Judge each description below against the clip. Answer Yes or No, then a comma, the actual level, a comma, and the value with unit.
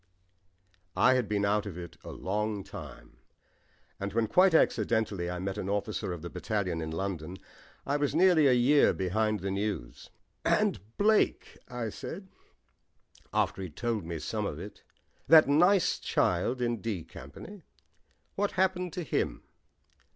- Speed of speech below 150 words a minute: No, average, 155 wpm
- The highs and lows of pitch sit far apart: Yes, wide, 7.3 semitones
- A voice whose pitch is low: Yes, low, 110 Hz